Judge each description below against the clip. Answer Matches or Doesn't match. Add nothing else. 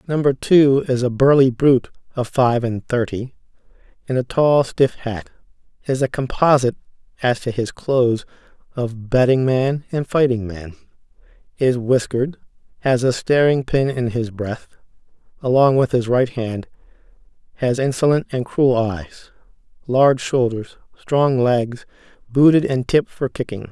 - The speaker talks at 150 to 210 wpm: Doesn't match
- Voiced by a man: Matches